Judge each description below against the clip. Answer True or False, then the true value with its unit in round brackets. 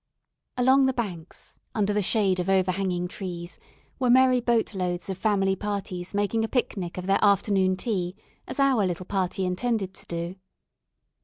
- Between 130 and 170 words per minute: True (160 wpm)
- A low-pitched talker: False (195 Hz)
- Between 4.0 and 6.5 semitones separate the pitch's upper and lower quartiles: False (3.5 semitones)